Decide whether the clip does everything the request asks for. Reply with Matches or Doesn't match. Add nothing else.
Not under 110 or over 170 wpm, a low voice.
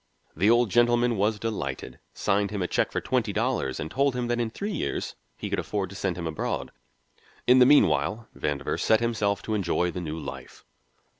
Doesn't match